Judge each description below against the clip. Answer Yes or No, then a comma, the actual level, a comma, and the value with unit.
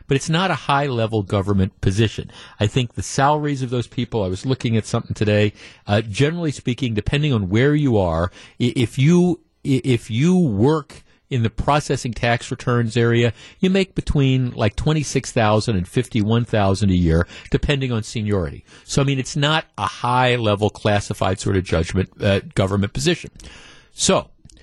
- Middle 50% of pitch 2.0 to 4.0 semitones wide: No, average, 4.9 semitones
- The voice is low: Yes, low, 120 Hz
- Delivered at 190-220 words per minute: No, average, 165 wpm